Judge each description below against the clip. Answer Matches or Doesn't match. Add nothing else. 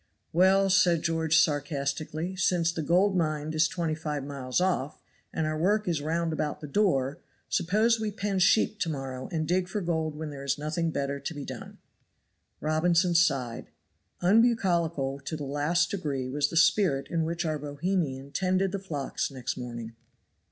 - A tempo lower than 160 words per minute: Doesn't match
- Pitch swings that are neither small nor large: Matches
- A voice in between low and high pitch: Matches